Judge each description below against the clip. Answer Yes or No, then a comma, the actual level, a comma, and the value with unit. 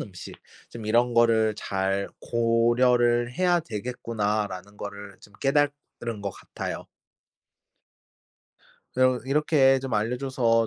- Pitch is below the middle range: Yes, low, 115 Hz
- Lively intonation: No, average, 3.5 semitones